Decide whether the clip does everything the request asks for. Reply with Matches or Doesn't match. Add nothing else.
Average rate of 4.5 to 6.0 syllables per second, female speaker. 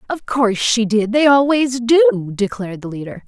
Matches